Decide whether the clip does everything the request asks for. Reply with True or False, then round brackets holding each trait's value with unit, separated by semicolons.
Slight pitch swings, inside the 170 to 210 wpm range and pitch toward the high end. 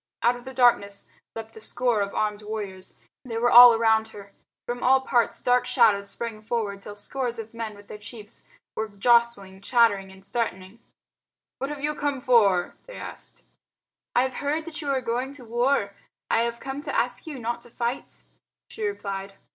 False (3.4 semitones; 185 wpm; 230 Hz)